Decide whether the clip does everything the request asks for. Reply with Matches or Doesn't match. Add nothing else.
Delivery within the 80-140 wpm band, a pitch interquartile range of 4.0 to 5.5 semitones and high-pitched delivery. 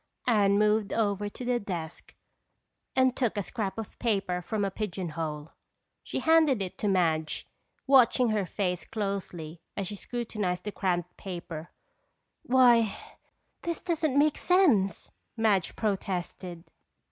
Matches